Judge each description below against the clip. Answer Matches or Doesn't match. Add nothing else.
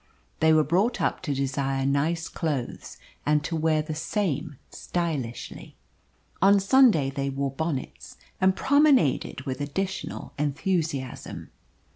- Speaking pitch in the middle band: Matches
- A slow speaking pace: Matches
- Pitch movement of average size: Matches